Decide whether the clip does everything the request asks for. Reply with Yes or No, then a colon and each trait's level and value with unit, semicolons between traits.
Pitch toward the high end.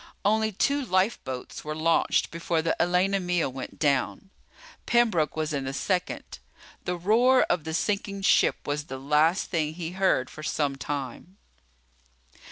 No: medium, 170 Hz